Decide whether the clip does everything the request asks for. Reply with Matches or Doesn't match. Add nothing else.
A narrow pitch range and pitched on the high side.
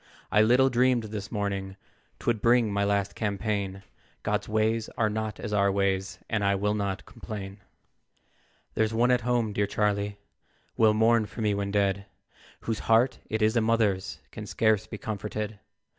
Doesn't match